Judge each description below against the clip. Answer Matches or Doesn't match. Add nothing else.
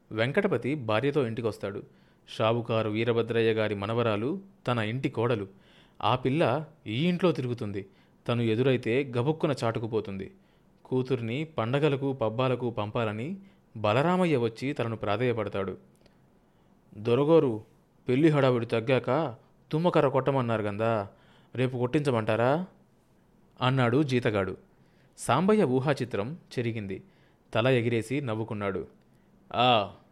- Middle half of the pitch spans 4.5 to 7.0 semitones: Doesn't match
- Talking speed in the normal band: Matches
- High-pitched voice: Doesn't match